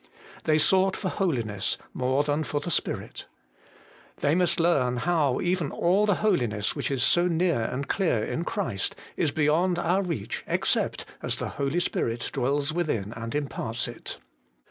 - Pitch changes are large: Yes, wide, 5.9 semitones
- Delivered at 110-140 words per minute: No, average, 160 wpm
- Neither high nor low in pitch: Yes, medium, 150 Hz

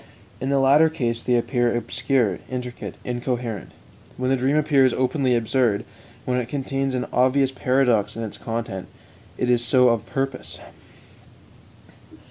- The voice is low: Yes, low, 125 Hz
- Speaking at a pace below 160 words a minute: Yes, average, 140 wpm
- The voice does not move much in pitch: Yes, narrow, 2.1 semitones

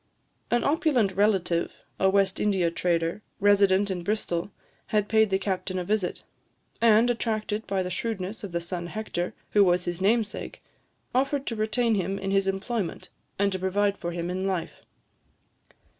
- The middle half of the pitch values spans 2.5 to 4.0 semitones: Yes, average, 2.9 semitones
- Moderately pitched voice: No, high, 195 Hz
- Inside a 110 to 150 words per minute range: No, average, 160 wpm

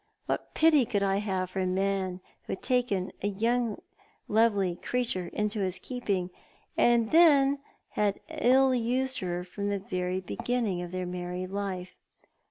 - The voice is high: Yes, high, 200 Hz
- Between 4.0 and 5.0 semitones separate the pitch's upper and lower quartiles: Yes, average, 4.6 semitones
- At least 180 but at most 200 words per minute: No, average, 150 wpm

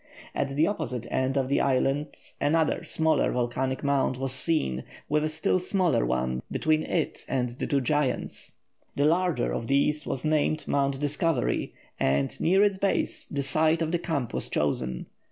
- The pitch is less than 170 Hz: Yes, medium, 140 Hz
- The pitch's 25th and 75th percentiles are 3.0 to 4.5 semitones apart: Yes, average, 3.8 semitones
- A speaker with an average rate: Yes, average, 170 wpm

